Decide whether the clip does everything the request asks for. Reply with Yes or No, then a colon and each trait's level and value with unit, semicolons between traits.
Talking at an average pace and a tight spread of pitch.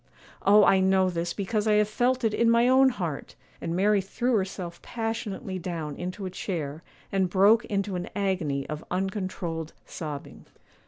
No: average, 165 wpm; average, 3.4 semitones